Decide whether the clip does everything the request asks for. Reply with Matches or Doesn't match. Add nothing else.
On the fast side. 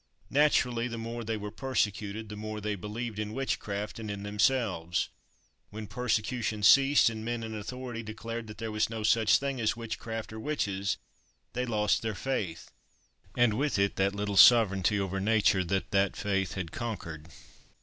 Doesn't match